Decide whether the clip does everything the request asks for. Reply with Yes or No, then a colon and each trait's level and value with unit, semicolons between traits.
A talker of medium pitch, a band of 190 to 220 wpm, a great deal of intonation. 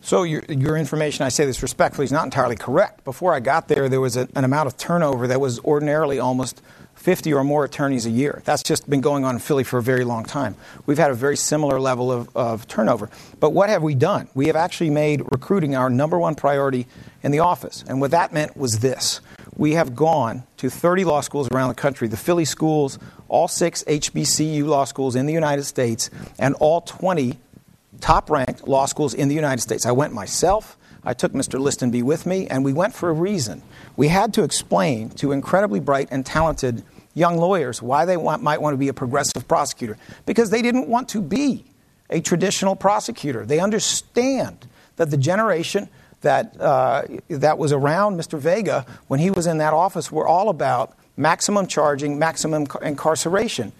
No: medium, 150 Hz; average, 200 wpm; average, 3.8 semitones